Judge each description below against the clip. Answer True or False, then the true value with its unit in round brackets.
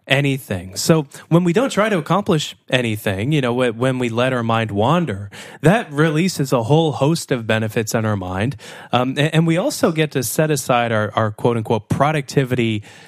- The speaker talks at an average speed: True (185 wpm)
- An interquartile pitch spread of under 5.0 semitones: False (5.5 semitones)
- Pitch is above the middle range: False (135 Hz)